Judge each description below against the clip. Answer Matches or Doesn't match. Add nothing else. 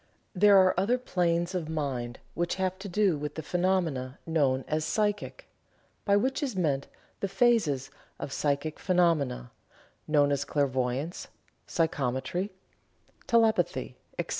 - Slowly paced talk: Matches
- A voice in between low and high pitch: Matches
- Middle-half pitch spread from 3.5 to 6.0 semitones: Matches